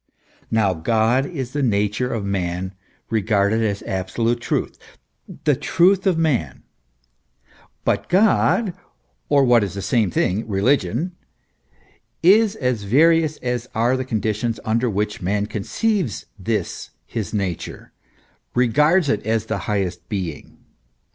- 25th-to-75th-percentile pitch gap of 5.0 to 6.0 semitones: Yes, wide, 5.5 semitones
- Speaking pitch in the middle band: No, low, 115 Hz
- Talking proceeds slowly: Yes, slow, 130 wpm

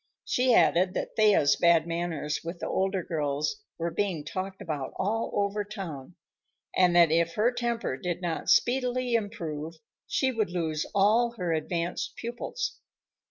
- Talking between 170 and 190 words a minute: No, average, 150 wpm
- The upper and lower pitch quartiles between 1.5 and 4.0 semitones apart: No, average, 4.8 semitones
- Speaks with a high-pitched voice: No, medium, 180 Hz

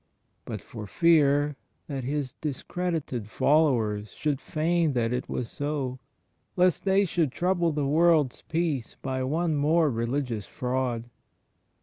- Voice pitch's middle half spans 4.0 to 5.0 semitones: Yes, average, 4.5 semitones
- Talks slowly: Yes, slow, 130 wpm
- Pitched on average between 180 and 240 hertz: No, medium, 145 Hz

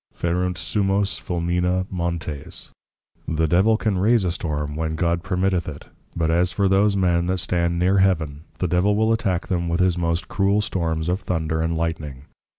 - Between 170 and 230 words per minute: Yes, average, 175 wpm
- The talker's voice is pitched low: Yes, very low, 90 Hz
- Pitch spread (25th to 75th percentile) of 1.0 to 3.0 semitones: Yes, narrow, 2.6 semitones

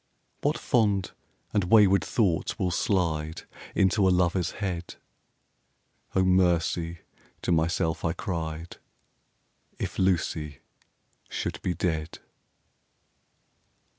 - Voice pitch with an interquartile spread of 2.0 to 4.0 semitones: Yes, narrow, 2.5 semitones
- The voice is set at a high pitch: No, very low, 90 Hz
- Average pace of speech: No, slow, 95 wpm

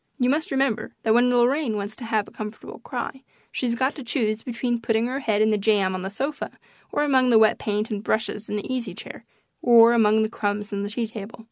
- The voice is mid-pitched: No, high, 225 Hz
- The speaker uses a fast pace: Yes, fast, 235 wpm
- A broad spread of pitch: No, average, 2.9 semitones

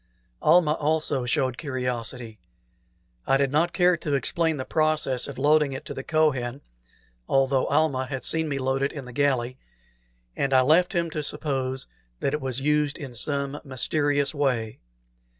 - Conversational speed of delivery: Yes, average, 165 wpm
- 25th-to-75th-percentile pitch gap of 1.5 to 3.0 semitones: Yes, average, 2.7 semitones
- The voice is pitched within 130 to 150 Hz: Yes, medium, 140 Hz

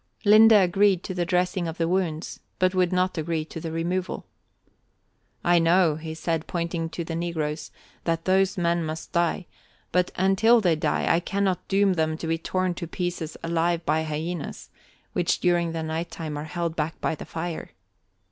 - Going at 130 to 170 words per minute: No, average, 180 wpm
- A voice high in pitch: No, medium, 170 Hz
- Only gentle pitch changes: Yes, narrow, 2.1 semitones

